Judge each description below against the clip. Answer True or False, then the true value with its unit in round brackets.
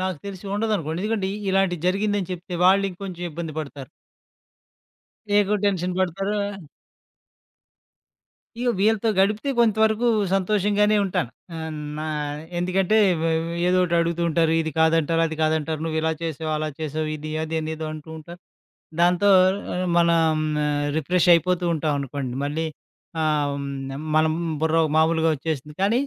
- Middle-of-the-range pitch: True (170 Hz)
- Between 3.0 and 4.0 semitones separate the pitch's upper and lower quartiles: True (3.5 semitones)